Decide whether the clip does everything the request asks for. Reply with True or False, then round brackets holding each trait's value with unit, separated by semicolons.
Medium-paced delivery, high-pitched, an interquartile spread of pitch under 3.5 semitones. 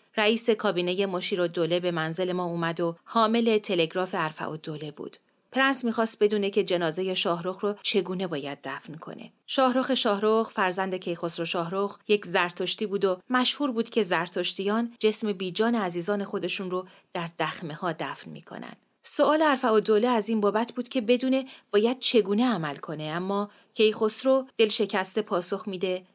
False (160 wpm; 200 Hz; 4.0 semitones)